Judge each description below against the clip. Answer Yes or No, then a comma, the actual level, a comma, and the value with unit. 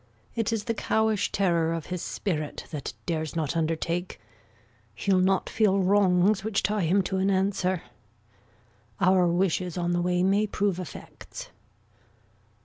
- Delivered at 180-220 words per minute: No, average, 140 wpm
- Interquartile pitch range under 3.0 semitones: Yes, narrow, 2.6 semitones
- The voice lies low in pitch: No, medium, 185 Hz